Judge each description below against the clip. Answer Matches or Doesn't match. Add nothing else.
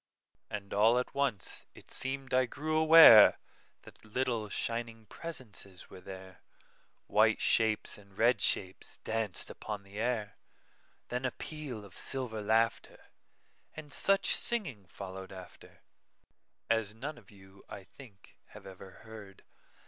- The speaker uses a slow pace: Matches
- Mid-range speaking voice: Doesn't match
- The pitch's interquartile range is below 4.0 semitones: Doesn't match